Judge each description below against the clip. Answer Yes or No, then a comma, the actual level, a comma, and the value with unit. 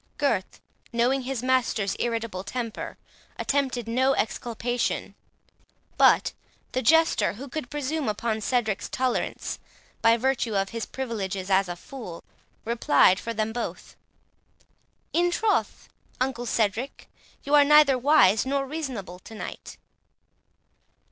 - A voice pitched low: No, high, 240 Hz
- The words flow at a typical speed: No, slow, 120 wpm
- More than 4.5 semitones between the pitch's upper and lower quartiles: No, average, 3.8 semitones